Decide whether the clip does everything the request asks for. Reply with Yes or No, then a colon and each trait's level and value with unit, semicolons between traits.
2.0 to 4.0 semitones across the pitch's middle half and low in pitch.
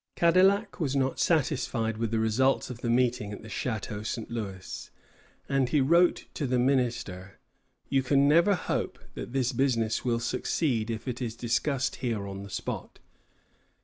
Yes: average, 3.6 semitones; low, 125 Hz